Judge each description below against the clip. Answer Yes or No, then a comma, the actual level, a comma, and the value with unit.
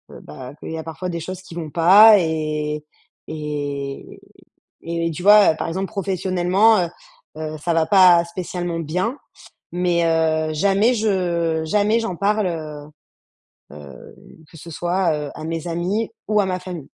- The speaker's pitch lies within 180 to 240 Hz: No, medium, 170 Hz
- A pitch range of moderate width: Yes, average, 3.2 semitones